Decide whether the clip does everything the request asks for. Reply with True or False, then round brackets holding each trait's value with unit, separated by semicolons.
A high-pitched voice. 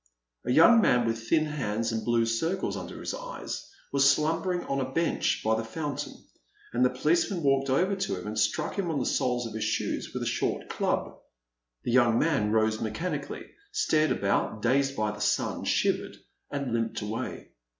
False (130 Hz)